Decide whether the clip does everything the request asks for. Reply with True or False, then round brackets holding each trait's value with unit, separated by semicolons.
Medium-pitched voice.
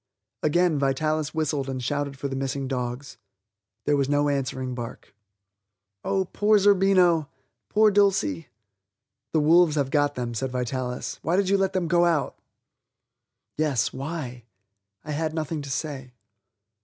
True (145 Hz)